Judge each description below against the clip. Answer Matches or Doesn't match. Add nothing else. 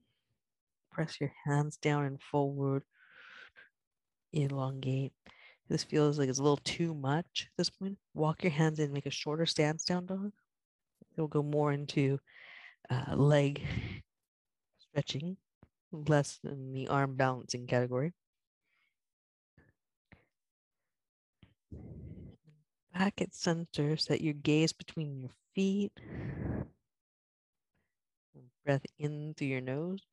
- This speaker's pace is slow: Matches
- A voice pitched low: Doesn't match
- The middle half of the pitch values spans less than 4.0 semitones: Matches